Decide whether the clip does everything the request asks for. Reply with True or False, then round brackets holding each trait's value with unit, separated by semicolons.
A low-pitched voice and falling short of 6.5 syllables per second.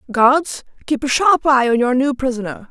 False (260 Hz; 4.9 syllables/s)